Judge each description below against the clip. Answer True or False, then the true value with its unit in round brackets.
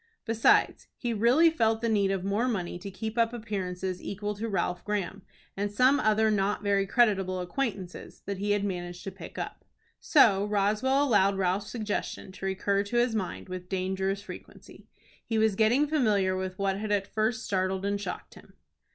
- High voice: True (205 Hz)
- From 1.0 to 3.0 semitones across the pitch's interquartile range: True (2.5 semitones)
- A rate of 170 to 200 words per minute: True (180 wpm)